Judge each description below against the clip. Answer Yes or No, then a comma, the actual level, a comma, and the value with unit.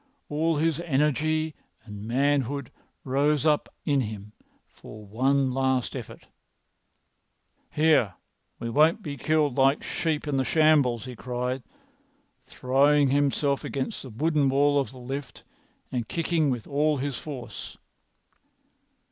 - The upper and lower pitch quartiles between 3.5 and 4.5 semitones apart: No, average, 2.9 semitones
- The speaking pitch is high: No, medium, 140 Hz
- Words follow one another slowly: Yes, slow, 125 wpm